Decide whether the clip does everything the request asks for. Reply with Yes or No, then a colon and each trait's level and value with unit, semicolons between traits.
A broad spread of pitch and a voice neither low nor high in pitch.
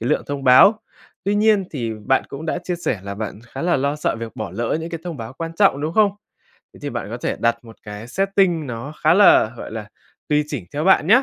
Yes: wide, 7.2 semitones; medium, 145 Hz